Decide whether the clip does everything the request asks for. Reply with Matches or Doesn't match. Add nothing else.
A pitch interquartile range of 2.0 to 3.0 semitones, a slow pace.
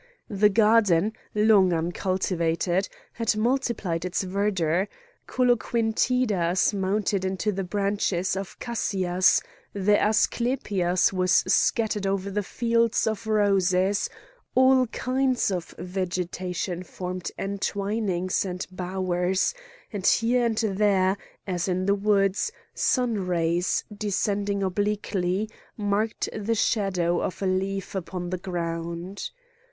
Matches